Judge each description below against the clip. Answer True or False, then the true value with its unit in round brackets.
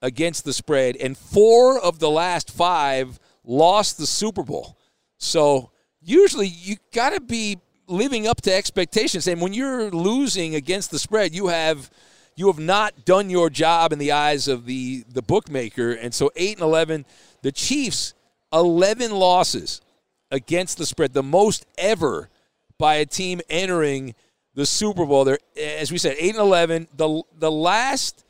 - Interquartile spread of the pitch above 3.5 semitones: True (5.0 semitones)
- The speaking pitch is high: False (170 Hz)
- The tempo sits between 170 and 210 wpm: False (160 wpm)